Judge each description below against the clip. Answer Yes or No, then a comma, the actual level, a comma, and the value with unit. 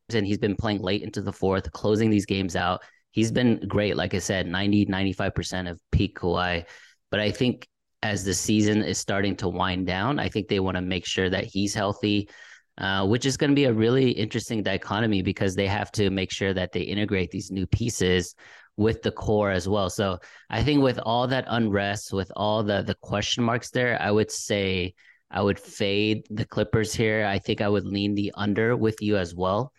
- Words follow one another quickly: Yes, fast, 210 wpm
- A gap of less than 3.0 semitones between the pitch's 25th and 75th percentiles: Yes, narrow, 2.4 semitones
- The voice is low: Yes, low, 100 Hz